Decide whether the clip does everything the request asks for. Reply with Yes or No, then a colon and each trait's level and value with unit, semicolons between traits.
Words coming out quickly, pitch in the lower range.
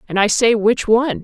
No: fast, 245 wpm; high, 225 Hz